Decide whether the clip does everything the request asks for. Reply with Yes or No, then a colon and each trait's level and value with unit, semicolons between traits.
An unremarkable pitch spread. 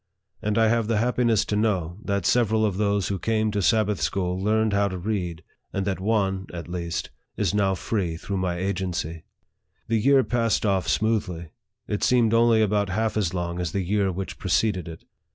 Yes: average, 3.3 semitones